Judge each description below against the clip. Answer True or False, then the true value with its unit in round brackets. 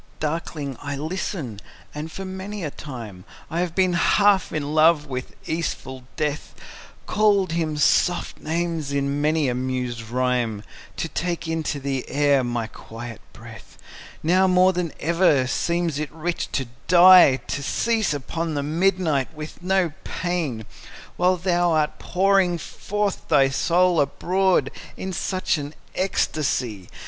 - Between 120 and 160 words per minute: True (140 wpm)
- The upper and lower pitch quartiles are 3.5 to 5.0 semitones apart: True (4.5 semitones)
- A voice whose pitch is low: False (160 Hz)